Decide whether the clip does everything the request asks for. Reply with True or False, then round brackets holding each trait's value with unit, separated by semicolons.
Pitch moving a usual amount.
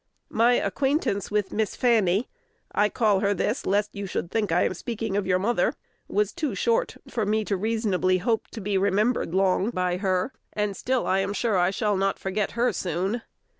True (3.0 semitones)